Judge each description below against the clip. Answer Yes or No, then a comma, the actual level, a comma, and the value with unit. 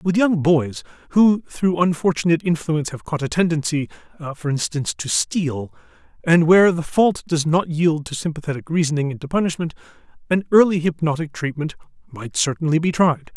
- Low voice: No, medium, 160 Hz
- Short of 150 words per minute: No, average, 160 wpm